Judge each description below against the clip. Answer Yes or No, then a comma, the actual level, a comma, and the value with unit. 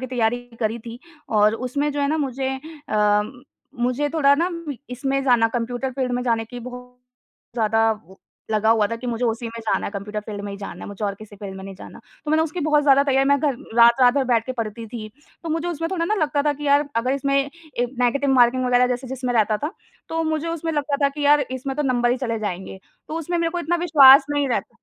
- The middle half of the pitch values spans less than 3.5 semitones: No, average, 4.2 semitones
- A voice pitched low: No, very high, 255 Hz